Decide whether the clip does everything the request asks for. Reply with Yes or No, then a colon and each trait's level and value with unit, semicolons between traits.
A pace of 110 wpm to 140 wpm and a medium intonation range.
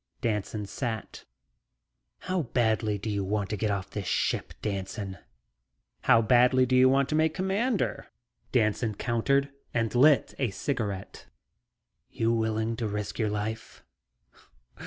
Yes: slow, 135 wpm; average, 3.7 semitones